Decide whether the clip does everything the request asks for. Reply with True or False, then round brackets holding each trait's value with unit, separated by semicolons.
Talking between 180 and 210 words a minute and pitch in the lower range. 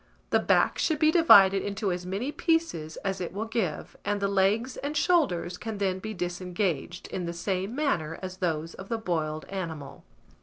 False (185 wpm; 190 Hz)